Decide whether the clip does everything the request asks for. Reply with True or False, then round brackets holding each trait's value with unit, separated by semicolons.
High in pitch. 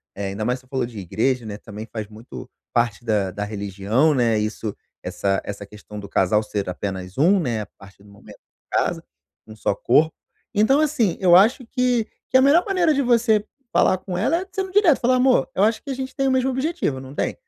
False (130 Hz)